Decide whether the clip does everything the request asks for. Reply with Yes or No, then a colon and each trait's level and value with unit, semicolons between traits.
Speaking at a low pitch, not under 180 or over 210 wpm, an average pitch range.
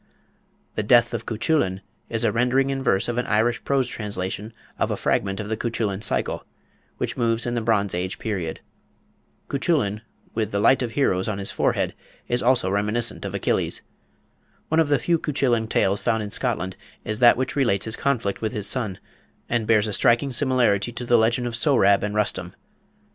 Yes: low, 115 Hz; average, 185 wpm; average, 3.3 semitones